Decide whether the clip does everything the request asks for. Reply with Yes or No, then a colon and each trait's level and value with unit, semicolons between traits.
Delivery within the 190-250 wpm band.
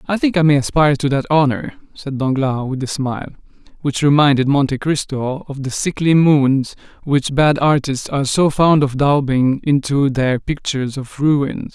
No: average, 175 wpm